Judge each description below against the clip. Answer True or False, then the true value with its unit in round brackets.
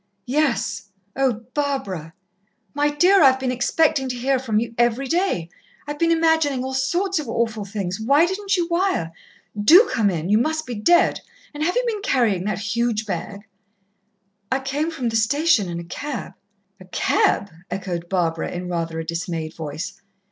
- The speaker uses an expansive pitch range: True (7.6 semitones)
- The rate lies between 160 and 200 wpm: True (170 wpm)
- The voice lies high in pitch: True (245 Hz)